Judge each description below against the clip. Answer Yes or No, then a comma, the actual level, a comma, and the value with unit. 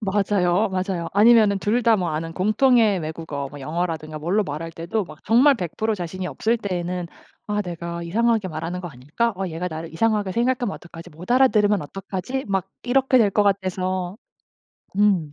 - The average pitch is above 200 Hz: No, high, 190 Hz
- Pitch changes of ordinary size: Yes, average, 4.2 semitones